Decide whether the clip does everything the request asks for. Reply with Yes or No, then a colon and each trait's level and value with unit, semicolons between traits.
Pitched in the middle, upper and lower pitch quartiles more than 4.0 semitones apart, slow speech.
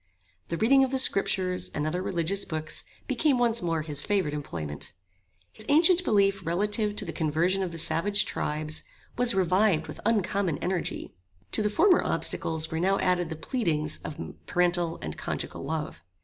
No: medium, 180 Hz; average, 4.7 semitones; average, 165 wpm